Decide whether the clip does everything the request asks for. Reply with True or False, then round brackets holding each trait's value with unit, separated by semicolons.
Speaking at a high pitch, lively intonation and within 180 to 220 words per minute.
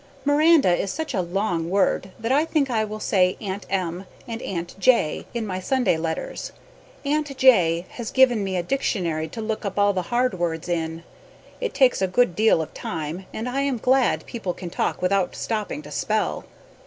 True (205 Hz; 6.1 semitones; 190 wpm)